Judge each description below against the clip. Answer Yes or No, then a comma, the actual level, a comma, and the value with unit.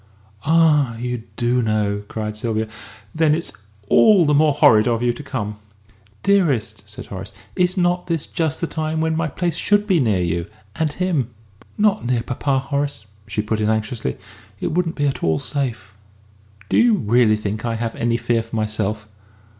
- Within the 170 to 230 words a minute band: Yes, average, 180 wpm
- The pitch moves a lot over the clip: Yes, wide, 6.7 semitones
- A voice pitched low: Yes, low, 125 Hz